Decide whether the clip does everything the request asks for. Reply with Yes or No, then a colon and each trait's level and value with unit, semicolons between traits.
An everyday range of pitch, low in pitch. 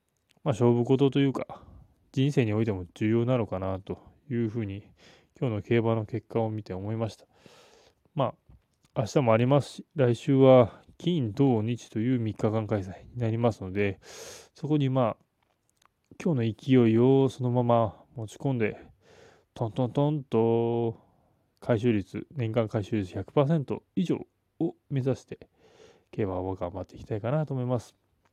Yes: average, 3.5 semitones; low, 115 Hz